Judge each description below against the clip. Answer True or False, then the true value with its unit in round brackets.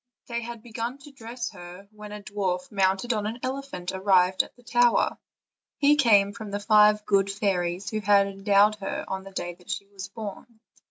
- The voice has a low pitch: False (205 Hz)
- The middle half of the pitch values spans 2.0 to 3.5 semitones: True (3.0 semitones)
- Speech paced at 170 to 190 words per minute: True (180 wpm)